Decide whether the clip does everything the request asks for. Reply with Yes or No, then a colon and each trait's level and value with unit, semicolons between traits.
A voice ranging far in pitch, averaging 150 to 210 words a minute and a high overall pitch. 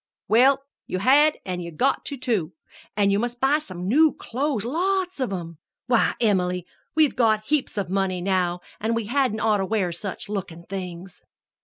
Yes: wide, 6.2 semitones; average, 175 wpm; high, 215 Hz